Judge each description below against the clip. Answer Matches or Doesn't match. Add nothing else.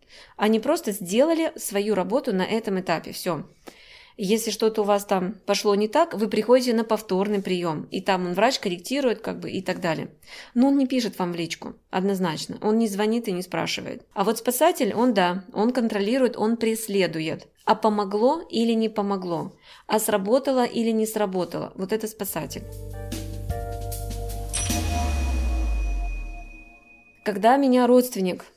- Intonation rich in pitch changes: Doesn't match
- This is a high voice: Matches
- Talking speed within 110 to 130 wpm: Doesn't match